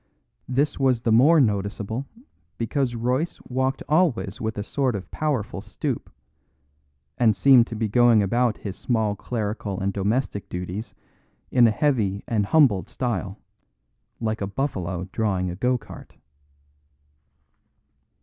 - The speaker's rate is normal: No, slow, 130 wpm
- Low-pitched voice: Yes, low, 115 Hz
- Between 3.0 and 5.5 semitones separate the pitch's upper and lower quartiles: Yes, average, 4.0 semitones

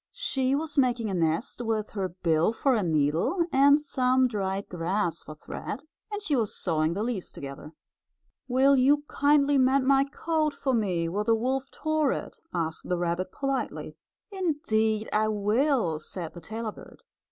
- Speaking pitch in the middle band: No, high, 225 Hz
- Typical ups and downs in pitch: No, wide, 7.3 semitones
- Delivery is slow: No, average, 165 wpm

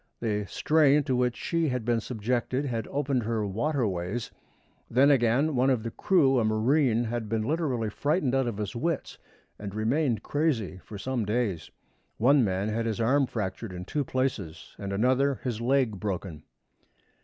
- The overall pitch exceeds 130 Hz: No, low, 120 Hz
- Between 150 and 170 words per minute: Yes, average, 165 wpm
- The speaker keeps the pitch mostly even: No, average, 4.1 semitones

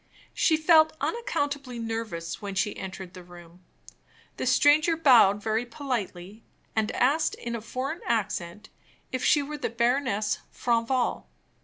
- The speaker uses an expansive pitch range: Yes, wide, 5.8 semitones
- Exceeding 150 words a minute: No, slow, 135 wpm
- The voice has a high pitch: Yes, high, 235 Hz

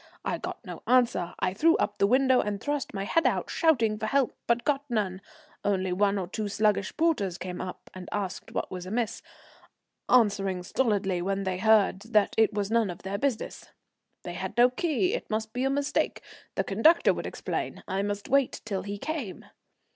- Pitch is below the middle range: No, high, 210 Hz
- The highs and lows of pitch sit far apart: No, average, 4.5 semitones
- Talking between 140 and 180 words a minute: No, average, 190 wpm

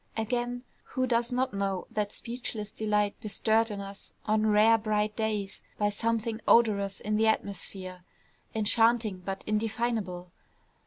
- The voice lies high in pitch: Yes, high, 215 Hz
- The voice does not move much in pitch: Yes, narrow, 2.1 semitones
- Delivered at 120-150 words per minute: Yes, slow, 135 wpm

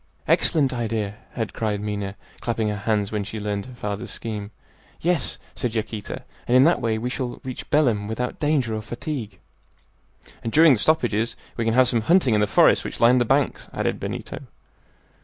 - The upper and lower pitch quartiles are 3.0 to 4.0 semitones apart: Yes, average, 3.4 semitones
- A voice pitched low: Yes, low, 115 Hz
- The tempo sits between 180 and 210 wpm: Yes, average, 185 wpm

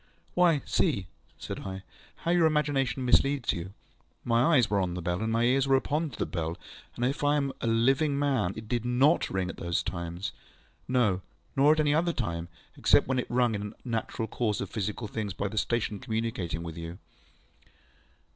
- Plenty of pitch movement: Yes, wide, 6.0 semitones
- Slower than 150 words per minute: No, fast, 205 wpm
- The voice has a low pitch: Yes, low, 115 Hz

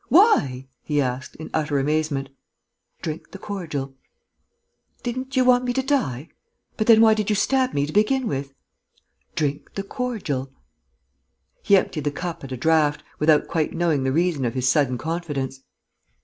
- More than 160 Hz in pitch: No, medium, 155 Hz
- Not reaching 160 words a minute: No, average, 165 wpm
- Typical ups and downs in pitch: No, wide, 7.7 semitones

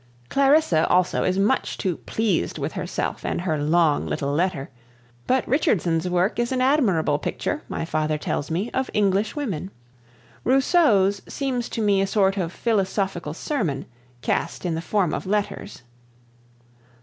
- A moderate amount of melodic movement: No, wide, 6.1 semitones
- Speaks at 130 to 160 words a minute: Yes, average, 150 wpm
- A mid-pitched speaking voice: No, high, 195 Hz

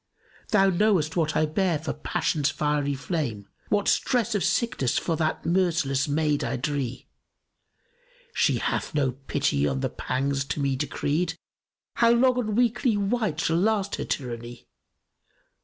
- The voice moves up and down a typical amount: No, wide, 6.3 semitones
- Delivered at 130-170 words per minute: Yes, average, 155 wpm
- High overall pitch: No, medium, 155 Hz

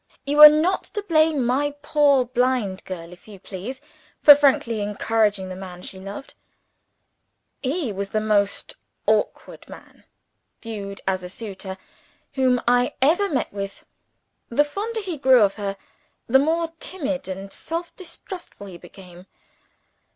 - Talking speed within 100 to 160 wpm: Yes, average, 145 wpm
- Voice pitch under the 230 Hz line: No, high, 240 Hz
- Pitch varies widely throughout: Yes, wide, 6.9 semitones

